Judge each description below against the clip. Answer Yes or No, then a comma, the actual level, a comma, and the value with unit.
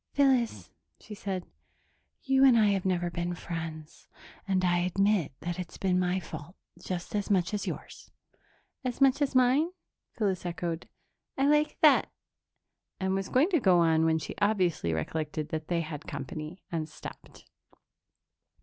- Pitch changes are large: No, average, 4.5 semitones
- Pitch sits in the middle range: Yes, medium, 180 Hz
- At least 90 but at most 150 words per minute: No, average, 160 wpm